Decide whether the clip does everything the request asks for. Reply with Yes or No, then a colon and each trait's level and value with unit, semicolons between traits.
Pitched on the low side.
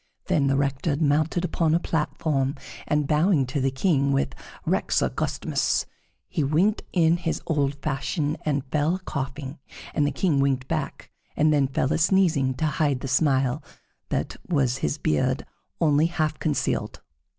No: medium, 145 Hz